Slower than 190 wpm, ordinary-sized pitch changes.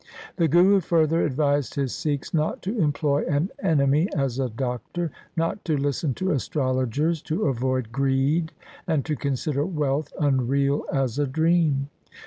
Yes: average, 145 wpm; average, 3.0 semitones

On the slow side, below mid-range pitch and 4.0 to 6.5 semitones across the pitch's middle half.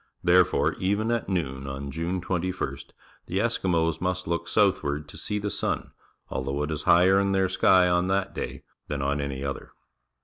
No: average, 175 wpm; very low, 90 Hz; average, 4.7 semitones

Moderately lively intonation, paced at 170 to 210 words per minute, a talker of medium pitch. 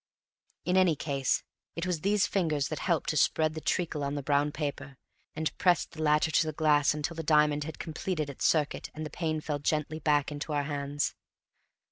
No: narrow, 1.7 semitones; average, 200 wpm; medium, 150 Hz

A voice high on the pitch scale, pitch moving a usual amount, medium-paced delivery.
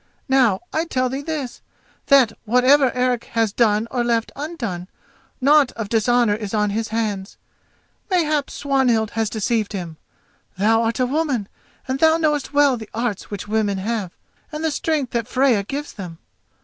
Yes: high, 235 Hz; average, 4.5 semitones; average, 160 wpm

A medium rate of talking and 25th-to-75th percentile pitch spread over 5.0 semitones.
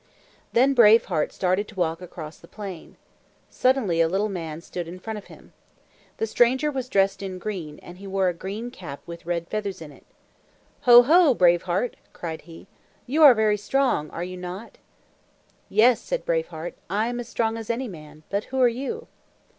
Yes: average, 195 wpm; wide, 5.6 semitones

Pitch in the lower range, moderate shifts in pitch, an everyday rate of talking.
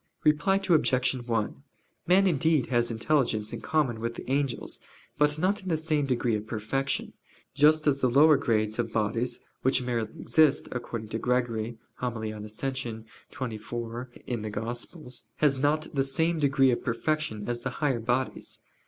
Yes: low, 125 Hz; average, 4.5 semitones; average, 160 wpm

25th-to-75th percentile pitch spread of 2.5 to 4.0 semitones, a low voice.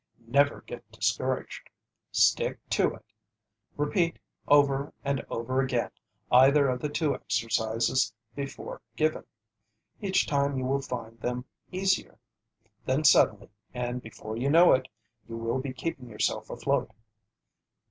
Yes: average, 3.3 semitones; low, 130 Hz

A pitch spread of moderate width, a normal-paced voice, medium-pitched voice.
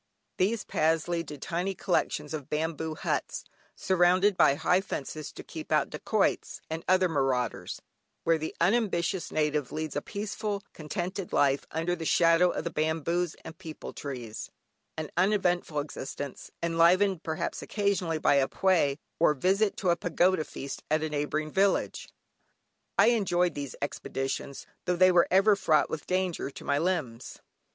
Yes: average, 3.5 semitones; average, 155 wpm; medium, 165 Hz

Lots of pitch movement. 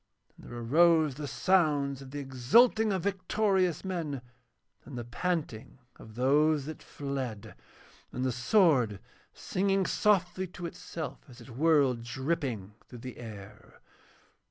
Yes: wide, 6.2 semitones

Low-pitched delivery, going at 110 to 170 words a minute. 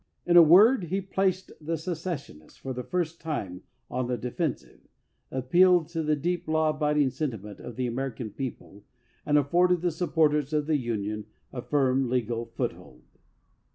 No: medium, 150 Hz; average, 160 wpm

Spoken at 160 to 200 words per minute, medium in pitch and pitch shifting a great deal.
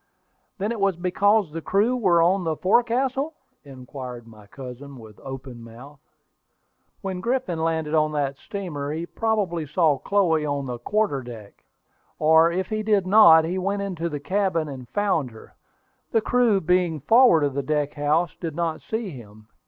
Yes: average, 170 wpm; medium, 165 Hz; wide, 5.9 semitones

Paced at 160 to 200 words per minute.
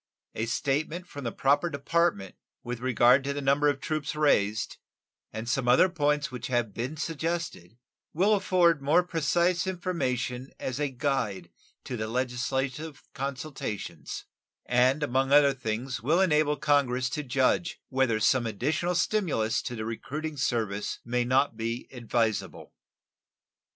No: average, 140 wpm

